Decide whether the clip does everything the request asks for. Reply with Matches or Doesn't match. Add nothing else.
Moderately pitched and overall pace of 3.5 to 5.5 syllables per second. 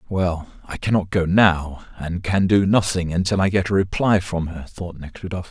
Doesn't match